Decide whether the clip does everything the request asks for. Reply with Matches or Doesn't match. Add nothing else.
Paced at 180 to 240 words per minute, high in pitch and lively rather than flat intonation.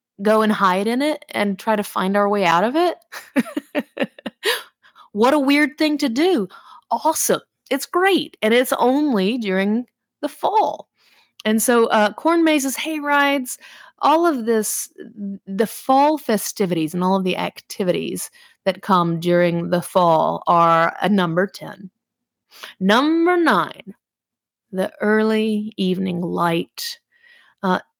Doesn't match